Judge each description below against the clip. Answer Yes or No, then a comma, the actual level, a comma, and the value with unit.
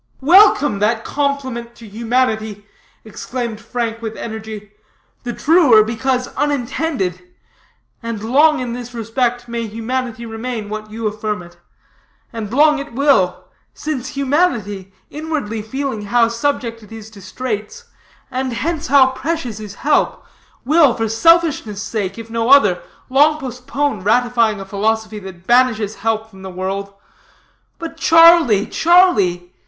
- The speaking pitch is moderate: No, high, 230 Hz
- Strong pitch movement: No, average, 4.2 semitones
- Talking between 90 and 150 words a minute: Yes, slow, 135 wpm